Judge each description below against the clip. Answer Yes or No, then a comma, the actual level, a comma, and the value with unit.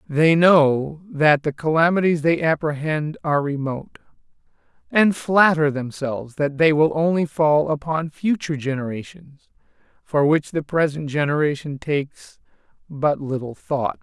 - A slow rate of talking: Yes, slow, 125 wpm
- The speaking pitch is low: No, medium, 150 Hz